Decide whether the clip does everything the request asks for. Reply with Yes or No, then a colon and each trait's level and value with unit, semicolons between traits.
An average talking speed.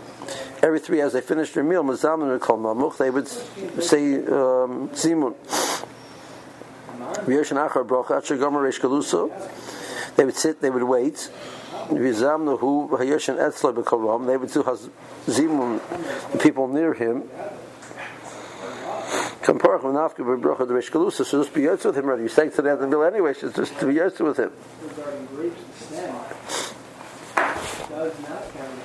No: slow, 90 wpm